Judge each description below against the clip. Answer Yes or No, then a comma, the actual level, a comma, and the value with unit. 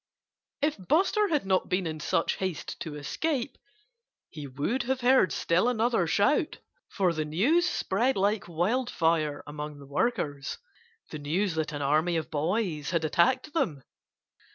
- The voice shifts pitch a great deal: Yes, wide, 7.9 semitones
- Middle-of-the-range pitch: Yes, medium, 180 Hz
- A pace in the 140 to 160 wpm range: Yes, average, 150 wpm